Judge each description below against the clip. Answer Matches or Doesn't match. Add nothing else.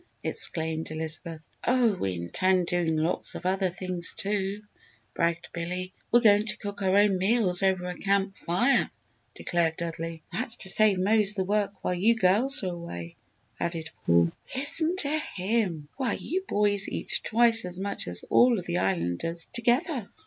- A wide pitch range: Doesn't match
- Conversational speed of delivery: Matches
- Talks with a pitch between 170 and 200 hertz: Matches